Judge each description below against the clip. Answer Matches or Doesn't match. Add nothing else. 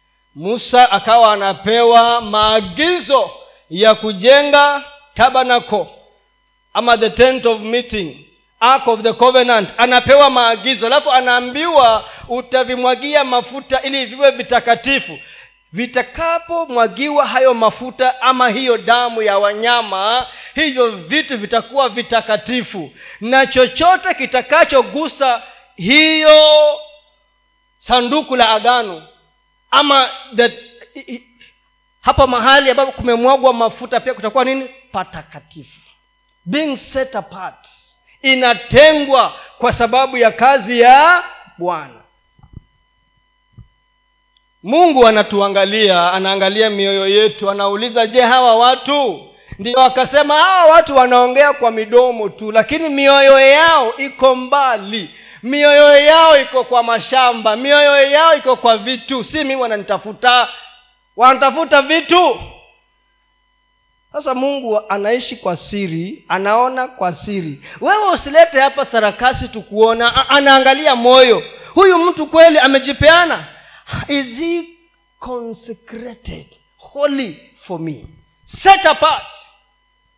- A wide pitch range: Doesn't match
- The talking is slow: Matches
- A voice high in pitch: Matches